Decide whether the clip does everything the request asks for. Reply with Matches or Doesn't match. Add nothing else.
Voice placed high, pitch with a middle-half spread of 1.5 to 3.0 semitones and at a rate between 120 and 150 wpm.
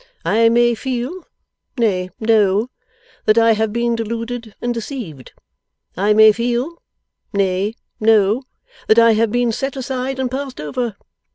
Matches